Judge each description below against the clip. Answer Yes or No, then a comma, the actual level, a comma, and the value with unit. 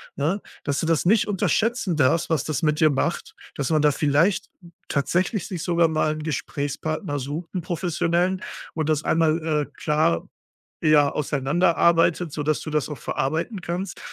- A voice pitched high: No, medium, 160 Hz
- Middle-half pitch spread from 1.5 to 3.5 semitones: Yes, narrow, 2.6 semitones